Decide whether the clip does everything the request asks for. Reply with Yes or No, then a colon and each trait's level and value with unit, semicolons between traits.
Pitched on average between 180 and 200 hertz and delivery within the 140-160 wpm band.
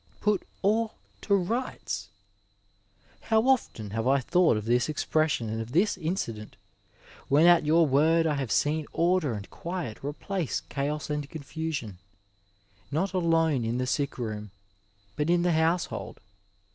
No: medium, 155 Hz; average, 150 wpm